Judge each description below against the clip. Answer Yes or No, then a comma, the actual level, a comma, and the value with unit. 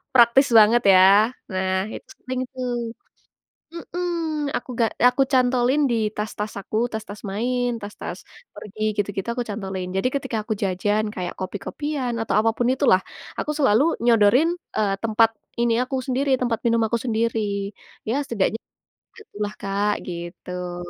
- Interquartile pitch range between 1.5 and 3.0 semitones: No, average, 3.7 semitones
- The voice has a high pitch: Yes, high, 225 Hz